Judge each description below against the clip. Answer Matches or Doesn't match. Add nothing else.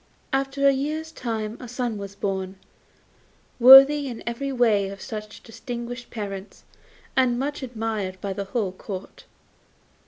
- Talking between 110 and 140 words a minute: Matches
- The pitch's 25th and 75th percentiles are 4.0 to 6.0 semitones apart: Matches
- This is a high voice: Matches